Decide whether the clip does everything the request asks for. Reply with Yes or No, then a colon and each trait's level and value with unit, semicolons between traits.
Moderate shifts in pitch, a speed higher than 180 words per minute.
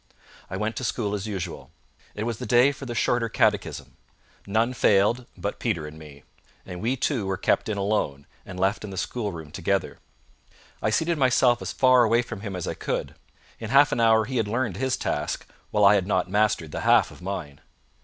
Yes: average, 4.0 semitones; fast, 205 wpm